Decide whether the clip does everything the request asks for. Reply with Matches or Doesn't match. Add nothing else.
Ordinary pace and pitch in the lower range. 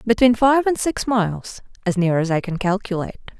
Doesn't match